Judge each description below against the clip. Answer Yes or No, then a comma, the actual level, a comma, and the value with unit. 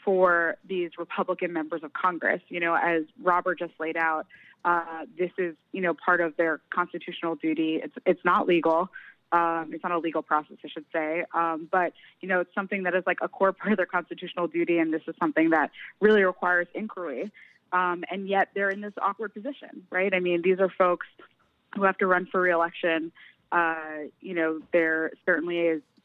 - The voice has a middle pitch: Yes, medium, 175 Hz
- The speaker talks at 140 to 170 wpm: No, average, 200 wpm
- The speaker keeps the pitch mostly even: Yes, narrow, 2.0 semitones